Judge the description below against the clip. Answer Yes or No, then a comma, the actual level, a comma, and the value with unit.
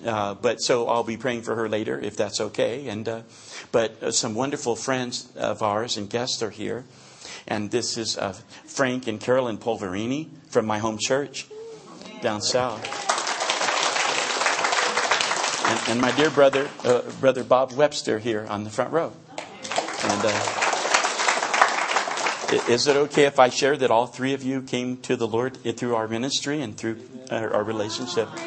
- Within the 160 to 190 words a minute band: Yes, average, 170 wpm